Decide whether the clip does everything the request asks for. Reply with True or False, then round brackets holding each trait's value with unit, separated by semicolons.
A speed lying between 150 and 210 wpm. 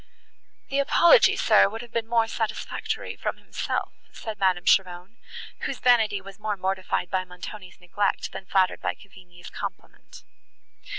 False (140 wpm)